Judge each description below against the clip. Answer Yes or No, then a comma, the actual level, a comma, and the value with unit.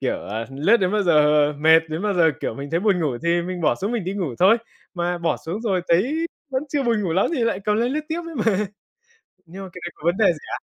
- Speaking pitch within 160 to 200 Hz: Yes, medium, 185 Hz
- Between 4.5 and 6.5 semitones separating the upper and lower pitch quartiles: Yes, average, 5.0 semitones